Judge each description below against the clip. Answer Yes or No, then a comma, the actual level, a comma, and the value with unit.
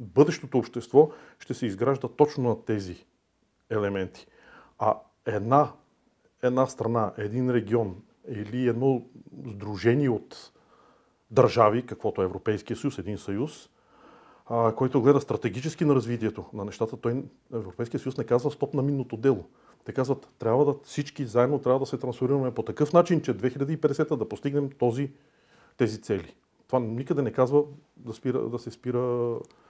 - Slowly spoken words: No, average, 145 wpm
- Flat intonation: No, average, 3.5 semitones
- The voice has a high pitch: No, low, 125 Hz